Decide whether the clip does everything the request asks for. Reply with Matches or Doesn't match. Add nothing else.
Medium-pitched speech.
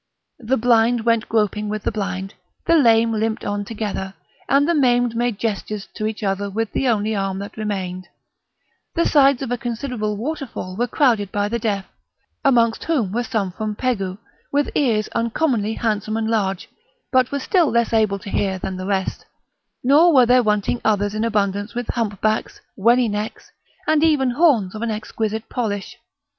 Doesn't match